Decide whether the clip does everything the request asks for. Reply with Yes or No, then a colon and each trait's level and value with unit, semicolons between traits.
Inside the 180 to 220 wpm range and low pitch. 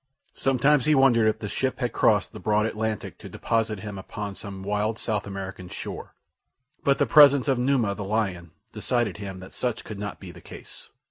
Yes: average, 195 wpm; low, 110 Hz